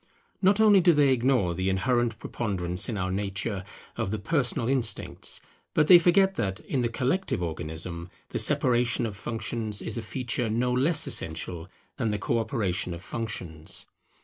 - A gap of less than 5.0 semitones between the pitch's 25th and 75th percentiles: No, wide, 5.4 semitones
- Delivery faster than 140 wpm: Yes, average, 165 wpm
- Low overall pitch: Yes, low, 115 Hz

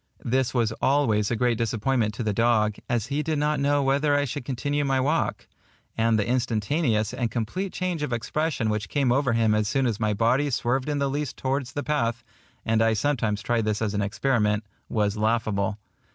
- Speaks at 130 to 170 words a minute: No, average, 200 wpm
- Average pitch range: Yes, average, 4.4 semitones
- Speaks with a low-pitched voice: Yes, low, 120 Hz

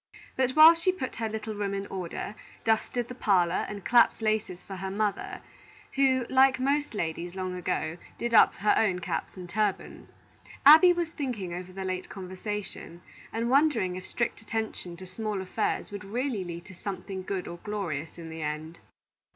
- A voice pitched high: Yes, high, 200 Hz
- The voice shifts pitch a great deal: No, average, 4.6 semitones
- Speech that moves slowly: No, average, 175 wpm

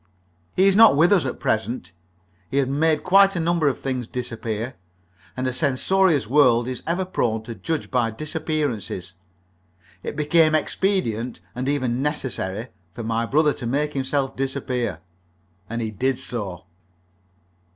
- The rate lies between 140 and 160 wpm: Yes, average, 150 wpm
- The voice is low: Yes, low, 130 Hz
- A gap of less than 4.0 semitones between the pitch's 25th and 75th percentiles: No, average, 4.9 semitones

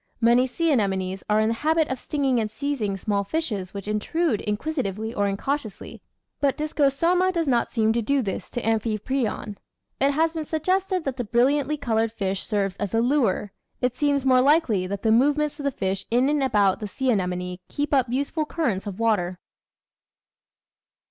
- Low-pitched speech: No, high, 240 Hz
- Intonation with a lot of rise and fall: Yes, wide, 5.8 semitones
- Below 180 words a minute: No, average, 185 wpm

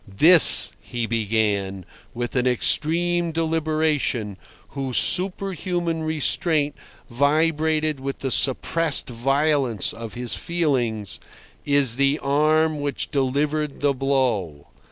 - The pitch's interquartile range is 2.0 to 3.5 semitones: No, average, 4.5 semitones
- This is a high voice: No, medium, 140 Hz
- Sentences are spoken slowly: Yes, slow, 100 wpm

